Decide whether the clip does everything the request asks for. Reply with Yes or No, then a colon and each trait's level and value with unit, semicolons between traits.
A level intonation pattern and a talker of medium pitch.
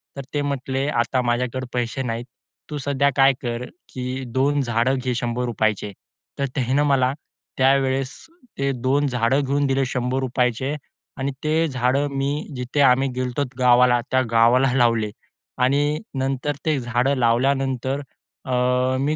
No: narrow, 1.9 semitones; low, 130 Hz